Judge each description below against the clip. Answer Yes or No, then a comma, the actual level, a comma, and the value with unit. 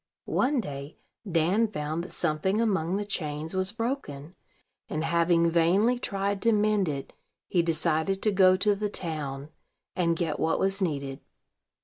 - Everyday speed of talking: Yes, average, 150 wpm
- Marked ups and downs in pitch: No, average, 4.4 semitones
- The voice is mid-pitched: Yes, medium, 175 Hz